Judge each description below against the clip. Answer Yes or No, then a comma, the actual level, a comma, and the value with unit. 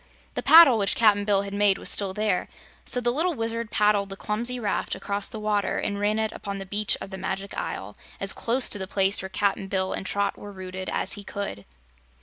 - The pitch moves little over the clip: Yes, narrow, 1.9 semitones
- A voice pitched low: No, high, 205 Hz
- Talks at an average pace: No, fast, 225 wpm